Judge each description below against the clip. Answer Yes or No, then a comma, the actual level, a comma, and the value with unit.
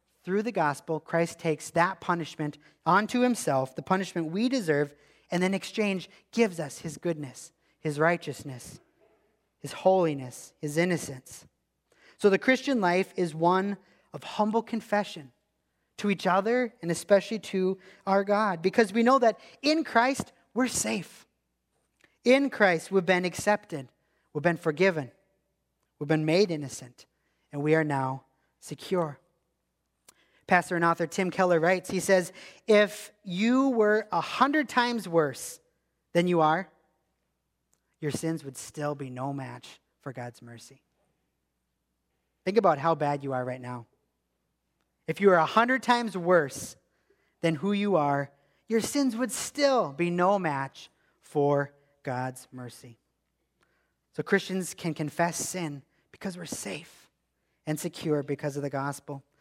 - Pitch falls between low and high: Yes, medium, 170 Hz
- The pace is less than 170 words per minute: Yes, average, 140 wpm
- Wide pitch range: Yes, wide, 5.7 semitones